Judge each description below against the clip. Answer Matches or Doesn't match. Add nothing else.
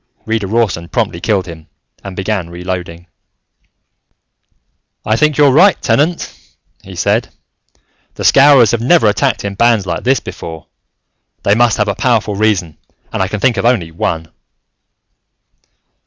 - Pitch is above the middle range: Doesn't match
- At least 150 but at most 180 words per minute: Doesn't match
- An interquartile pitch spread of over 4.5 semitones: Matches